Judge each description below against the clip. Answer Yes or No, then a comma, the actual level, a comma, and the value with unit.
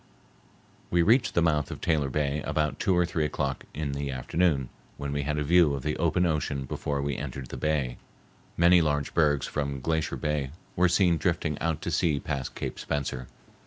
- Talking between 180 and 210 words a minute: Yes, average, 195 wpm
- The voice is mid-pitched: No, very low, 75 Hz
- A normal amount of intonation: Yes, average, 3.0 semitones